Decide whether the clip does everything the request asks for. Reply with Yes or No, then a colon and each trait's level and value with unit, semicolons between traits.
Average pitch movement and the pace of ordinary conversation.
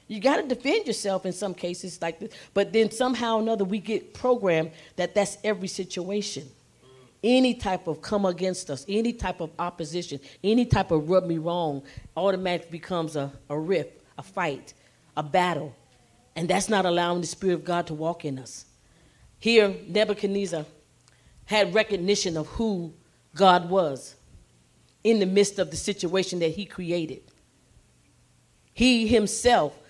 Yes: average, 4.3 semitones; average, 155 wpm